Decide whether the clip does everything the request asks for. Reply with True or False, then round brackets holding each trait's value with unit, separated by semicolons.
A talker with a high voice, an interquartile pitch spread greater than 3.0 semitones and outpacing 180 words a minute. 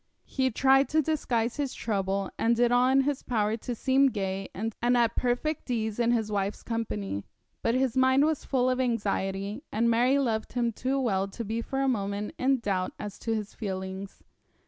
True (230 Hz; 4.0 semitones; 190 wpm)